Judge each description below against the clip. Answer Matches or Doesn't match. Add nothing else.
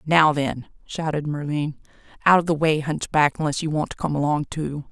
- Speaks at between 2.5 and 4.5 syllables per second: Doesn't match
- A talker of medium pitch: Matches